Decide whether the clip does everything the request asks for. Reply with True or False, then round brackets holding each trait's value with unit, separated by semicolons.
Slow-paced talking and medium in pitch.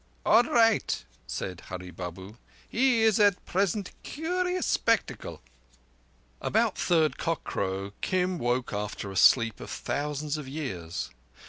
True (120 wpm; 150 Hz)